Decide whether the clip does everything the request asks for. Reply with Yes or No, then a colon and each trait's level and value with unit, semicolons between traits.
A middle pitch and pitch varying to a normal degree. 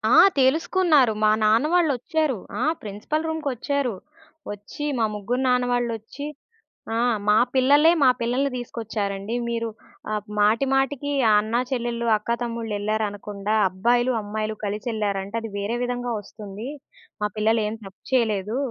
No: high, 230 Hz; average, 3.5 semitones